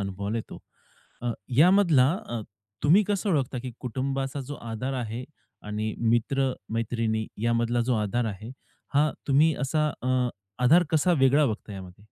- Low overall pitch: Yes, low, 125 Hz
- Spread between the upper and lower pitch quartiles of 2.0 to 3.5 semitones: No, average, 4.2 semitones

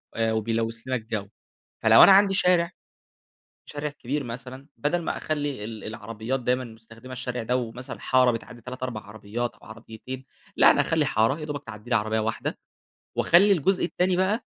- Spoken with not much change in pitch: No, average, 4.6 semitones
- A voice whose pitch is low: Yes, low, 125 Hz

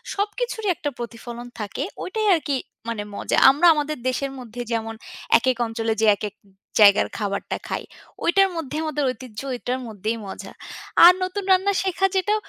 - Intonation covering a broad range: Yes, wide, 8.5 semitones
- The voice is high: Yes, very high, 260 Hz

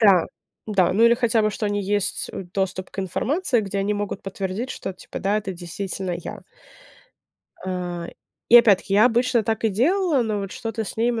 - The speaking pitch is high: Yes, high, 205 Hz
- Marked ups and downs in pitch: No, average, 3.2 semitones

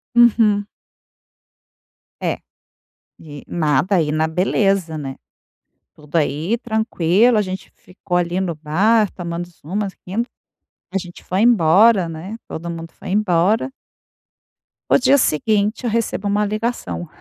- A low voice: No, medium, 185 Hz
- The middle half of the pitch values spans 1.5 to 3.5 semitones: No, average, 4.5 semitones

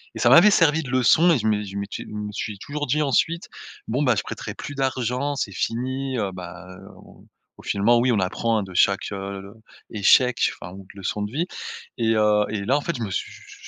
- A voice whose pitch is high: No, low, 115 Hz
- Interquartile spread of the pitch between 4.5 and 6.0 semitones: Yes, average, 5.2 semitones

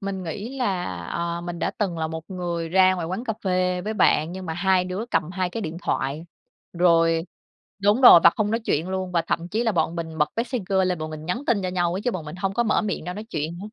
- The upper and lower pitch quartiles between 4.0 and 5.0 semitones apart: No, average, 3.0 semitones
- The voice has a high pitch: No, medium, 180 Hz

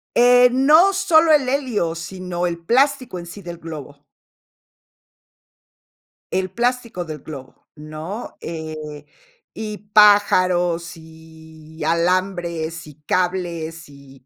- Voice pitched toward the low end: No, medium, 175 Hz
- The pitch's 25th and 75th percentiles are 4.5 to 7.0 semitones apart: Yes, average, 5.0 semitones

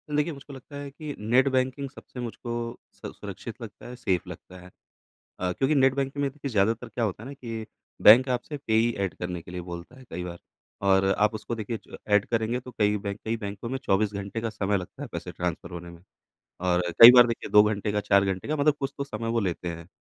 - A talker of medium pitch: No, low, 110 Hz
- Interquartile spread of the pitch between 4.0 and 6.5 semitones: Yes, average, 5.0 semitones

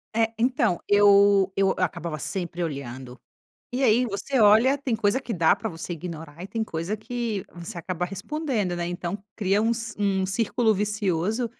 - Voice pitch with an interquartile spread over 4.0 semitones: Yes, average, 4.4 semitones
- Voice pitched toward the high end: Yes, high, 200 Hz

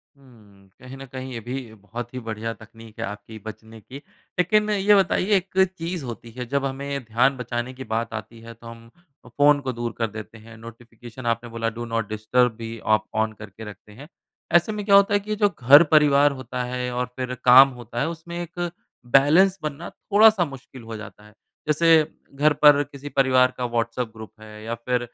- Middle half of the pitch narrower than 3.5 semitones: No, average, 4.1 semitones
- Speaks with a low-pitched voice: Yes, low, 125 Hz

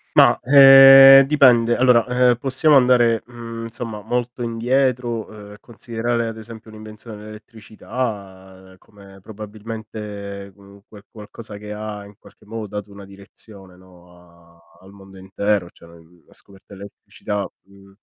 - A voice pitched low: Yes, low, 105 Hz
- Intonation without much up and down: No, average, 3.0 semitones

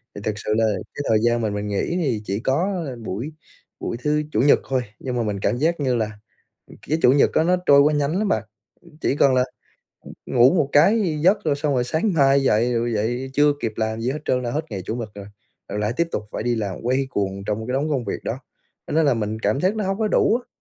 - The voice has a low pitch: Yes, low, 130 Hz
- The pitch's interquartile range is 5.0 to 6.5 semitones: Yes, wide, 5.4 semitones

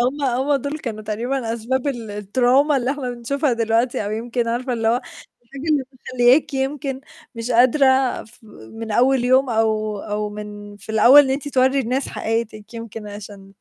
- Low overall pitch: No, high, 240 Hz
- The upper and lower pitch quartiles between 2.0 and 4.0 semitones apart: Yes, average, 3.3 semitones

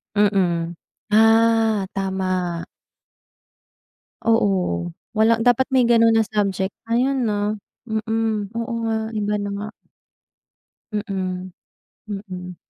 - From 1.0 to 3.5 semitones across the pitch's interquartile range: Yes, average, 3.0 semitones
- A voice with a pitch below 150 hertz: No, high, 210 Hz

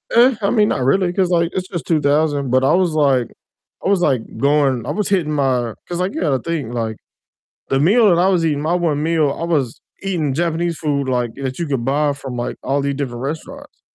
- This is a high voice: No, medium, 150 Hz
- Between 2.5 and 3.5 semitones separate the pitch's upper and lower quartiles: No, average, 4.4 semitones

